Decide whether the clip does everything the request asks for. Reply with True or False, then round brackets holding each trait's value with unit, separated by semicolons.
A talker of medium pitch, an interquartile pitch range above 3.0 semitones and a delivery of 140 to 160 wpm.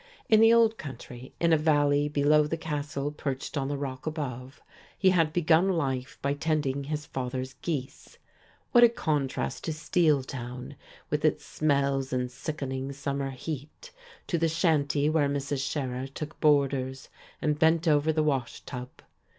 False (145 Hz; 2.7 semitones; 155 wpm)